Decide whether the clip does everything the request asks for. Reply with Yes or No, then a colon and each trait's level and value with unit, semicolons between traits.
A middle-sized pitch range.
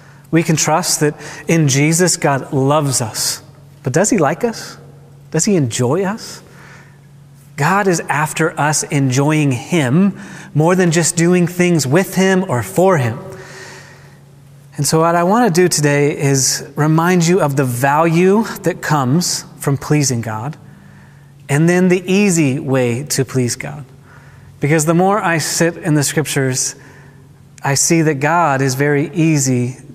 Yes: average, 3.4 semitones